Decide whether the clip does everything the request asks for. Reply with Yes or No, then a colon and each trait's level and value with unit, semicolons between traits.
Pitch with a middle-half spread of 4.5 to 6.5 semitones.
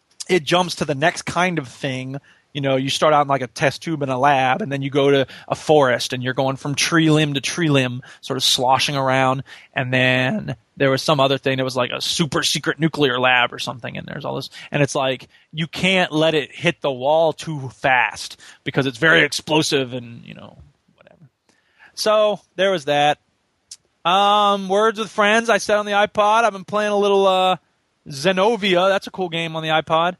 Yes: average, 5.1 semitones